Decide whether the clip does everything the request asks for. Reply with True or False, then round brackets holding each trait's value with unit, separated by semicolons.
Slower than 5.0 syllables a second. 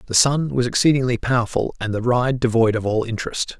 False (5.9 syllables/s)